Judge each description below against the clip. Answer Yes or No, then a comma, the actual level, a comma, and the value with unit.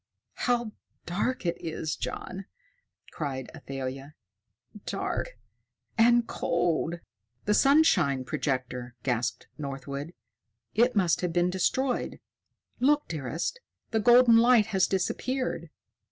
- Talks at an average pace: No, slow, 100 wpm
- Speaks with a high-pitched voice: No, medium, 175 Hz